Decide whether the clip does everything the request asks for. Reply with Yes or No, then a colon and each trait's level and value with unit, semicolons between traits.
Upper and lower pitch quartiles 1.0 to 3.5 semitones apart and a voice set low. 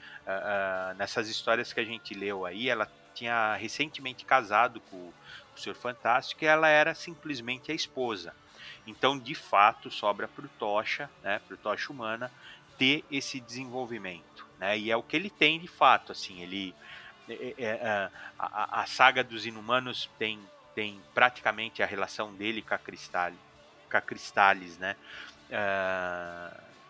No: average, 5.0 semitones; low, 110 Hz